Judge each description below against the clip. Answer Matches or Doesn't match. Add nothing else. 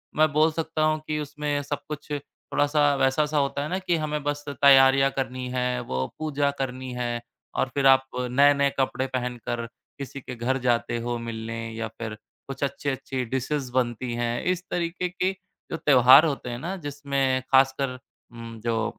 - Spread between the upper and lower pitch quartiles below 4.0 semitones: Matches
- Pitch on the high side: Doesn't match